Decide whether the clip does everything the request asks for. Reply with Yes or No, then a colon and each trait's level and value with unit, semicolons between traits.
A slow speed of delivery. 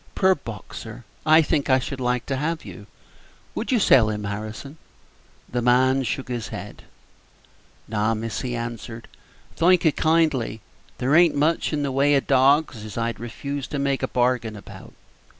No: average, 170 wpm